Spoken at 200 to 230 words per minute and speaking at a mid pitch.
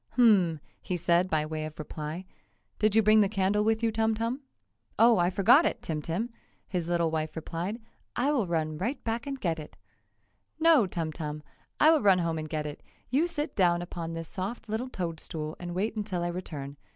Yes: fast, 205 wpm; medium, 180 Hz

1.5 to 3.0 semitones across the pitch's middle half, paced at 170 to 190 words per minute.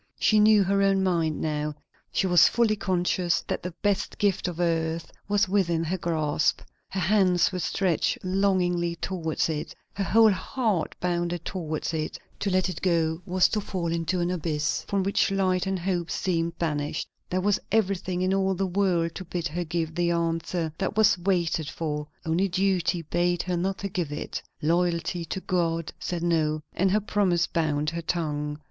Yes: narrow, 2.5 semitones; average, 180 wpm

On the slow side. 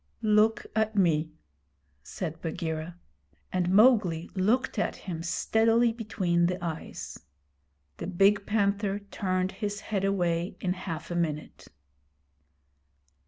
Yes: slow, 115 wpm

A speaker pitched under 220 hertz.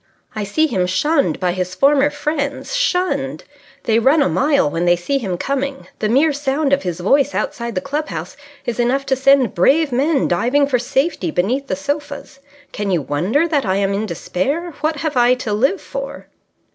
No: very high, 270 Hz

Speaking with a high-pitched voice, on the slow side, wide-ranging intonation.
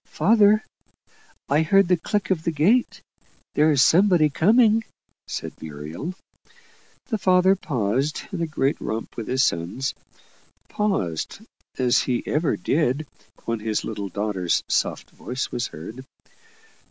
No: medium, 150 Hz; slow, 130 wpm; wide, 8.8 semitones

